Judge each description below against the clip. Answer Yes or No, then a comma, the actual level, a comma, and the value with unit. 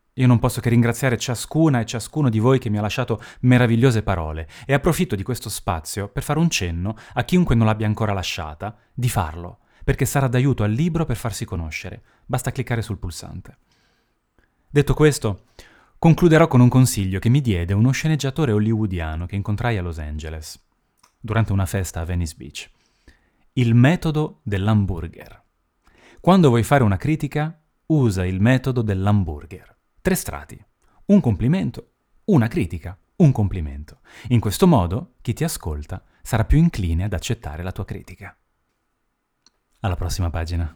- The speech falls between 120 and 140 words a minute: No, average, 155 wpm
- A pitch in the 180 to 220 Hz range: No, low, 110 Hz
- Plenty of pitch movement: Yes, wide, 6.1 semitones